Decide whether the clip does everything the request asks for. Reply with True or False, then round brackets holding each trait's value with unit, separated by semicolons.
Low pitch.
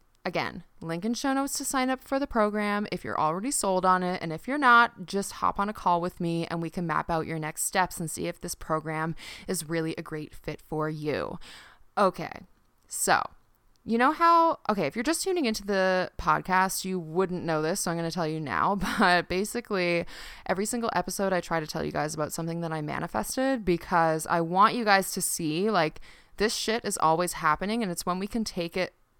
False (185 Hz)